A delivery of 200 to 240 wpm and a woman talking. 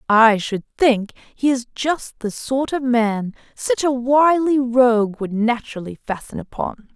No: average, 155 wpm; female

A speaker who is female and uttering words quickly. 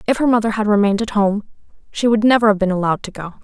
Yes: female; fast, 260 wpm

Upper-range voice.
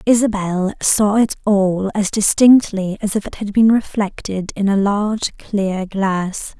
Yes: high, 200 Hz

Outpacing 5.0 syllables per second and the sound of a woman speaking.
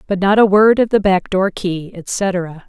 No: 4.0 syllables/s; female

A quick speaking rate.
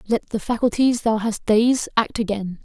No: average, 180 wpm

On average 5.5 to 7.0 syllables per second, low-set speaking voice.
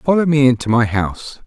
Yes: 5.7 syllables/s; low, 130 Hz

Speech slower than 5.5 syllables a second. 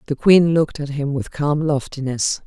Yes: 4.9 syllables/s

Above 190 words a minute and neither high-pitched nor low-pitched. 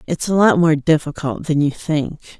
Yes: average, 200 wpm; medium, 155 Hz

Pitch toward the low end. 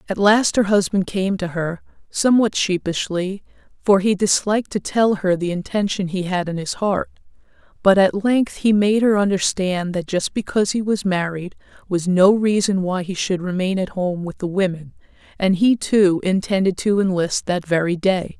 No: high, 190 Hz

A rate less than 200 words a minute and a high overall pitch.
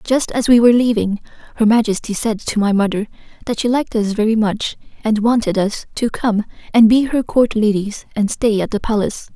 No: fast, 205 wpm; high, 220 Hz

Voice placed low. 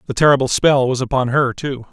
Yes: low, 130 Hz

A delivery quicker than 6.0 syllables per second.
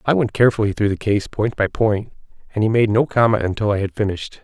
Yes: 6.4 syllables/s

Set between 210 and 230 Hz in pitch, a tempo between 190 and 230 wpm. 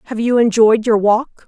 Yes: high, 225 Hz; fast, 205 wpm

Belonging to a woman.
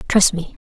Yes: female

